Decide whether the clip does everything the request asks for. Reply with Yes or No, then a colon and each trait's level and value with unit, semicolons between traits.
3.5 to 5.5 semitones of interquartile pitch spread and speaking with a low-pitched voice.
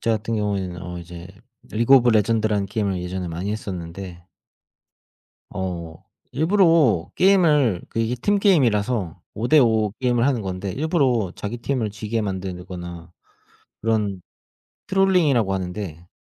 Yes: average, 5.1 semitones; low, 105 Hz